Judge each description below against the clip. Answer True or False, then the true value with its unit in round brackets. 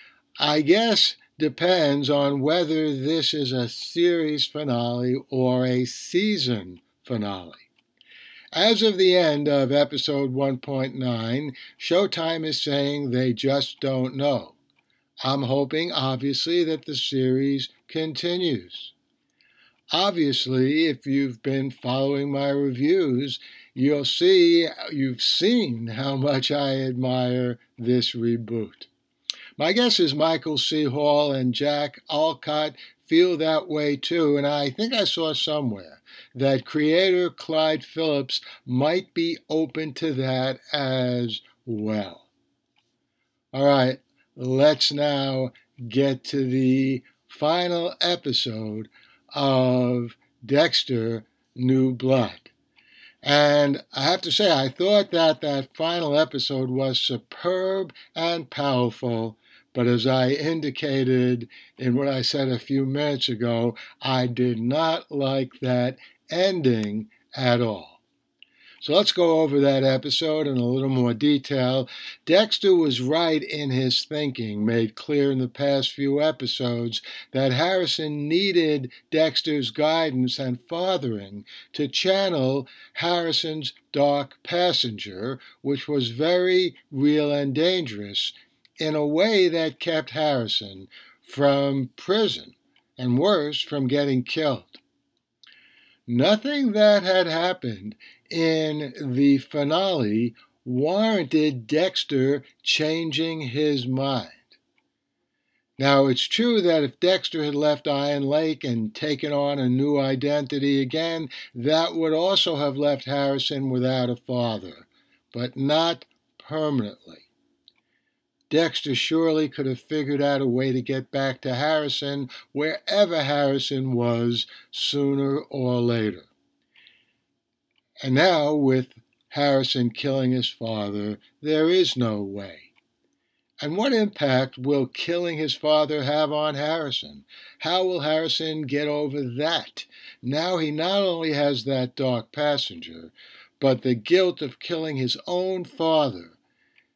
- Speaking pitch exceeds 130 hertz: True (140 Hz)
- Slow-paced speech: True (120 wpm)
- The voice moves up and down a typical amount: True (3.5 semitones)